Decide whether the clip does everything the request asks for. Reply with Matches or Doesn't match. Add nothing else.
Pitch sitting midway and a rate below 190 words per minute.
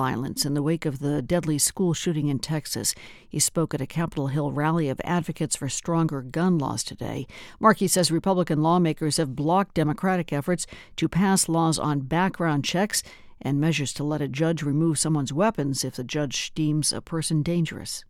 Matches